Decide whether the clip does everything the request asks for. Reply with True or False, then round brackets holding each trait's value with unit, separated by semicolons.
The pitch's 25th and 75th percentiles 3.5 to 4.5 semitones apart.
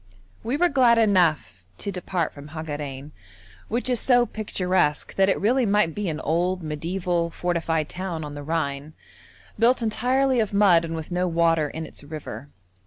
False (5.2 semitones)